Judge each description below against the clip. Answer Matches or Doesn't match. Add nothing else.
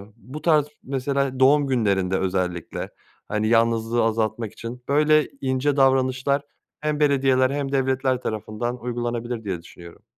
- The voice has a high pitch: Doesn't match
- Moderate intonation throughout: Matches